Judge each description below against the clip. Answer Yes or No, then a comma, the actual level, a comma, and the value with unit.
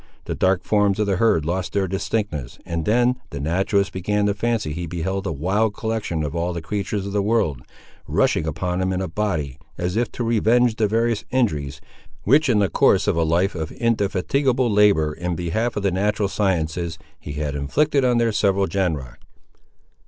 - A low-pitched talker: Yes, very low, 95 Hz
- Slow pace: No, average, 190 wpm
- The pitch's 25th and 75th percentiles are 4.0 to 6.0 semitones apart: Yes, average, 4.6 semitones